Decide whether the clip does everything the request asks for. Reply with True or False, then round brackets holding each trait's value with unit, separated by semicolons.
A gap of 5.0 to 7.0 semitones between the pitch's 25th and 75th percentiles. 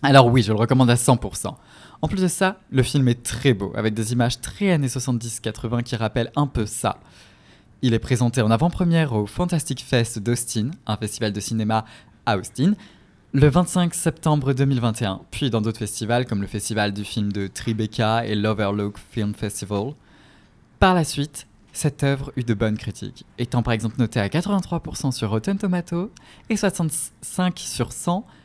True (5.4 semitones)